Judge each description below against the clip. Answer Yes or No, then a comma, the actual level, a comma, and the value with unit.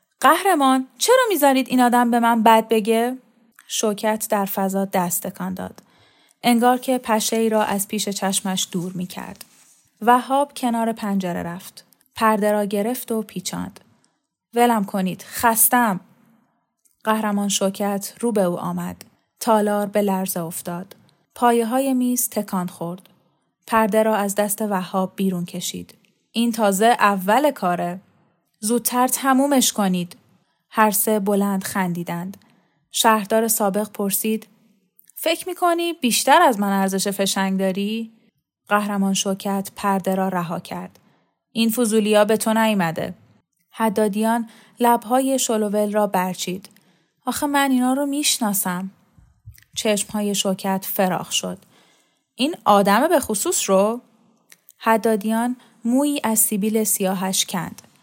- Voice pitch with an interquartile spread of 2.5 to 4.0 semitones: Yes, average, 3.4 semitones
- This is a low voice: No, high, 210 Hz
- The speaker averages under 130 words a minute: Yes, average, 120 wpm